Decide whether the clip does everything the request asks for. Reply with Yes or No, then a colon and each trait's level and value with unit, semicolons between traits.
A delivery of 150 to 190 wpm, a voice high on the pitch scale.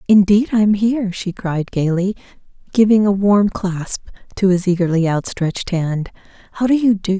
Yes: average, 160 wpm; high, 195 Hz